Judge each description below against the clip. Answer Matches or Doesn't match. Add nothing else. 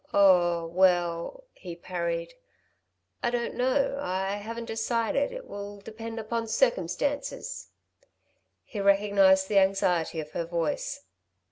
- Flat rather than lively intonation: Doesn't match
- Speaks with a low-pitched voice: Doesn't match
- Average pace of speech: Doesn't match